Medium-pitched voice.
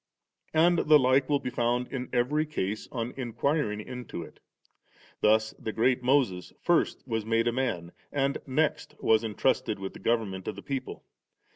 No: low, 120 Hz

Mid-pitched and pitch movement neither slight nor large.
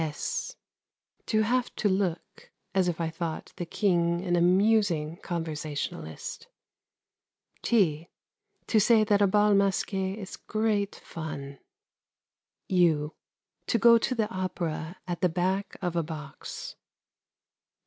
Yes: medium, 180 Hz; average, 4.0 semitones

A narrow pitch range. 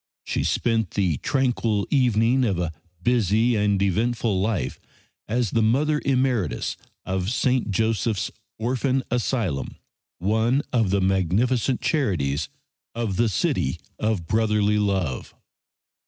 No: average, 4.1 semitones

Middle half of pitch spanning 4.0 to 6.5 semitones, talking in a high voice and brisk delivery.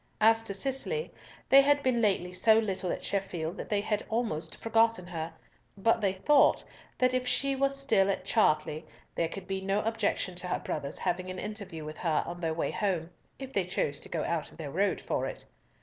Yes: average, 4.7 semitones; high, 195 Hz; fast, 210 wpm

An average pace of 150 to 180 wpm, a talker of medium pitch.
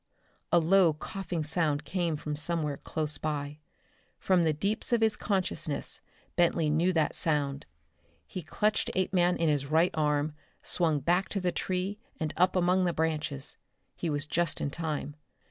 Yes: average, 160 wpm; medium, 165 Hz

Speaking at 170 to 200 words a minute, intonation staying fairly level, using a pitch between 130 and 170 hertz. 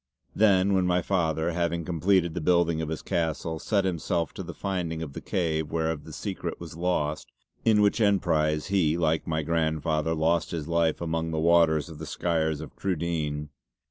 No: average, 180 wpm; narrow, 2.1 semitones; very low, 80 Hz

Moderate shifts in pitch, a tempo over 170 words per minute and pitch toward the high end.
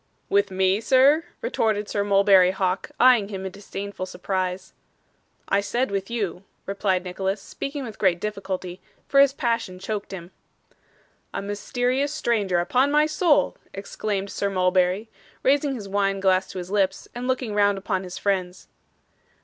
No: average, 4.1 semitones; average, 150 wpm; high, 200 Hz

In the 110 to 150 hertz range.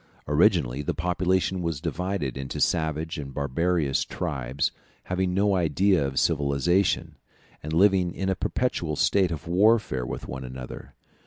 No: very low, 85 Hz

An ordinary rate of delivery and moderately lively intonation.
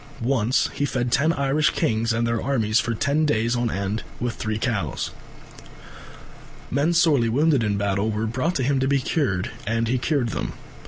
Yes: average, 180 wpm; average, 4.1 semitones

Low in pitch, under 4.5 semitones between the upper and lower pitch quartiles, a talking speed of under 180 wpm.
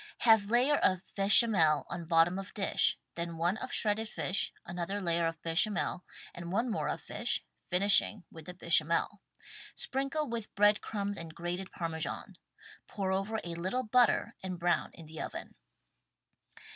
No: high, 190 Hz; average, 4.0 semitones; average, 160 wpm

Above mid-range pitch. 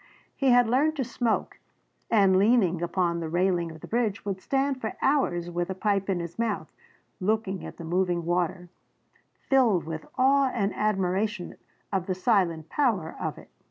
Yes: high, 195 Hz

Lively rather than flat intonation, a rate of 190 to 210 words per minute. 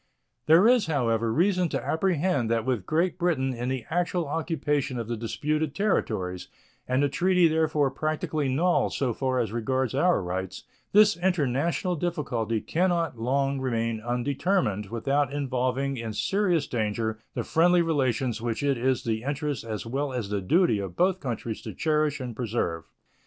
No: wide, 5.9 semitones; average, 160 wpm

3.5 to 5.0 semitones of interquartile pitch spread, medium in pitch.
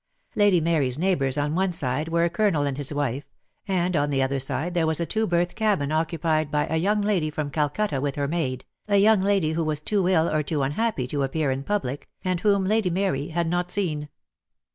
Yes: average, 4.4 semitones; medium, 160 Hz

